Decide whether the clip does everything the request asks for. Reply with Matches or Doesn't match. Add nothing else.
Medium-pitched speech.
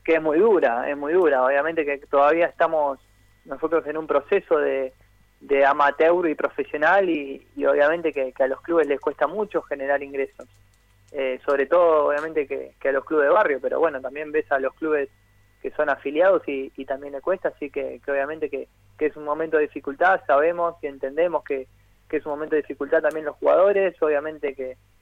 Matches